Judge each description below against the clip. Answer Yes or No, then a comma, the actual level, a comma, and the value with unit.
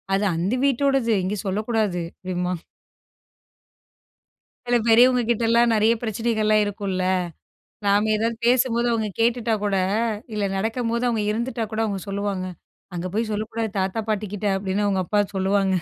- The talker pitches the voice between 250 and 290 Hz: No, high, 215 Hz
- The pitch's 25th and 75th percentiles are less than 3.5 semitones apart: Yes, average, 2.7 semitones